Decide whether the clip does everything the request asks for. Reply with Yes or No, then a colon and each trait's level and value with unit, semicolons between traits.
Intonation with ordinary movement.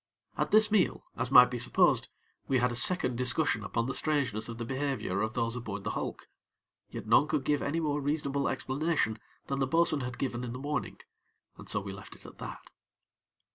Yes: average, 4.0 semitones